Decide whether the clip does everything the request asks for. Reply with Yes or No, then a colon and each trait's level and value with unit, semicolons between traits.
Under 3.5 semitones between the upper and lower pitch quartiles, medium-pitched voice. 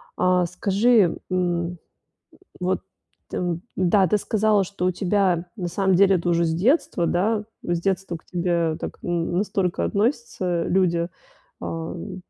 Yes: narrow, 2.4 semitones; medium, 180 Hz